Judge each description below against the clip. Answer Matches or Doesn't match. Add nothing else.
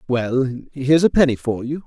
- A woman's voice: Doesn't match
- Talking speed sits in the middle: Matches